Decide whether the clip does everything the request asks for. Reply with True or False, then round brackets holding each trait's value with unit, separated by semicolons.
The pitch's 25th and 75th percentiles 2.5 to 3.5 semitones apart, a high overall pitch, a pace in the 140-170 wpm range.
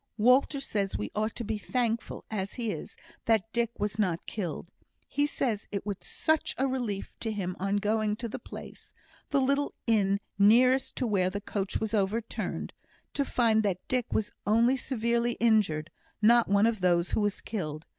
False (3.0 semitones; 220 Hz; 180 wpm)